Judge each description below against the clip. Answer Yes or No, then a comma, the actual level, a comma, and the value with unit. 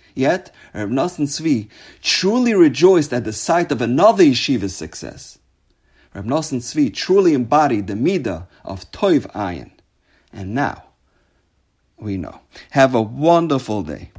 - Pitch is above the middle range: No, low, 135 Hz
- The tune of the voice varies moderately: No, wide, 9.0 semitones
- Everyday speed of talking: No, slow, 125 wpm